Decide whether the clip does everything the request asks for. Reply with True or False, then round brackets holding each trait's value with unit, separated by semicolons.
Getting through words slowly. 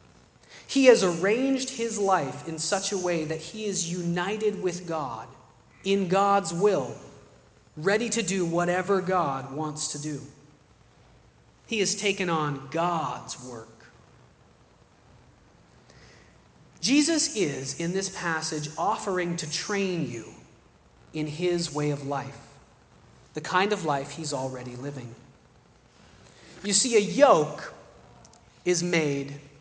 True (120 wpm)